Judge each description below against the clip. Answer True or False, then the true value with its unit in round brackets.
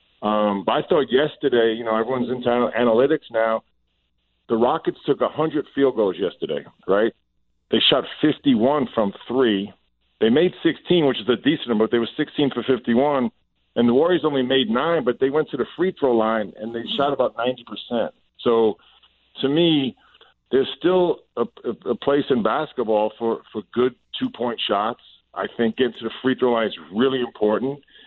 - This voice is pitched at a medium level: False (120 Hz)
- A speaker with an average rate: True (180 wpm)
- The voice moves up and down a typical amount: True (4.0 semitones)